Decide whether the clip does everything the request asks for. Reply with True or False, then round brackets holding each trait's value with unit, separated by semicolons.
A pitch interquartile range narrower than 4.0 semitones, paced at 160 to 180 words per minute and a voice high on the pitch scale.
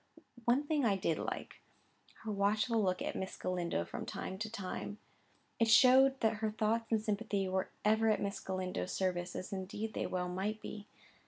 True (3.0 semitones; 175 wpm; 210 Hz)